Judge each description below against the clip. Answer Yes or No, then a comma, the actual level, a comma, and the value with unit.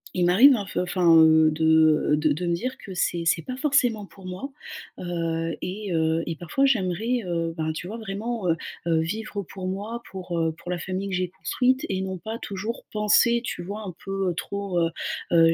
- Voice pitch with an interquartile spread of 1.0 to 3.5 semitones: No, average, 4.2 semitones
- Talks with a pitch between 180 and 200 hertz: Yes, medium, 185 Hz